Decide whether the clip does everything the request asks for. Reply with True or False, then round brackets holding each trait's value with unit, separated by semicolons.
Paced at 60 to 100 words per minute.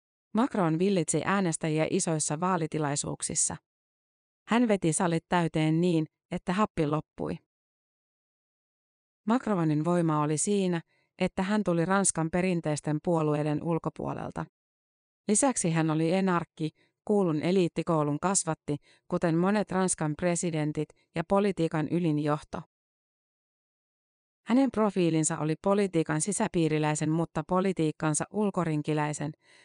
True (95 wpm)